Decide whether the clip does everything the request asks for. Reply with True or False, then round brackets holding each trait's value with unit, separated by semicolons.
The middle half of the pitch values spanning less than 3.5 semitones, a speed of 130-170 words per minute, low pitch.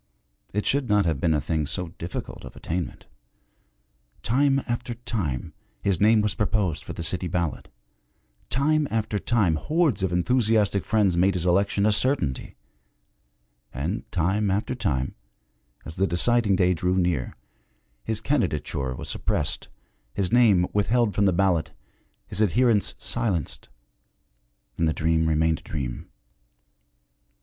False (5.2 semitones; 140 wpm; 95 Hz)